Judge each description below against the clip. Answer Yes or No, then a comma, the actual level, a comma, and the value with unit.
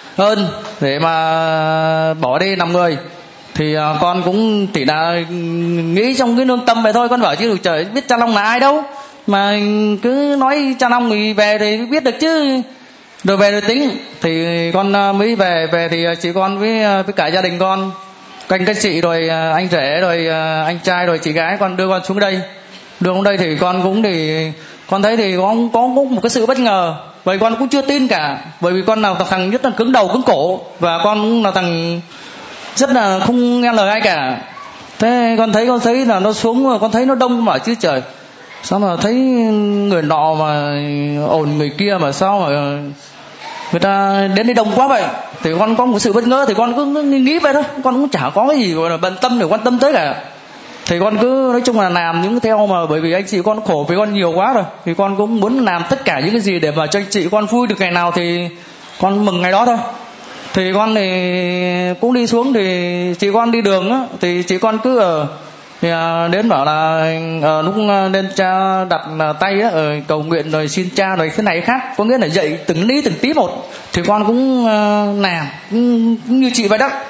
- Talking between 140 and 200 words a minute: No, average, 220 wpm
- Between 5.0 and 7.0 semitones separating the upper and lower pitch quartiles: Yes, average, 5.3 semitones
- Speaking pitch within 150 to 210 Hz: Yes, high, 200 Hz